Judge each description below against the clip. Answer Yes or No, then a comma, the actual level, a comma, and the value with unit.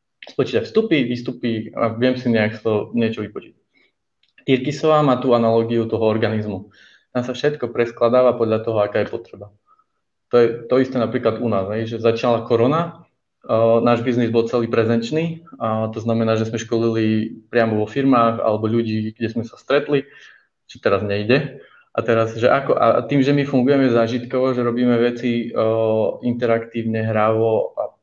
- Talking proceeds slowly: No, fast, 165 wpm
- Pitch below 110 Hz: No, low, 115 Hz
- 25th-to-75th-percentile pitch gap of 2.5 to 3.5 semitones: No, narrow, 2.1 semitones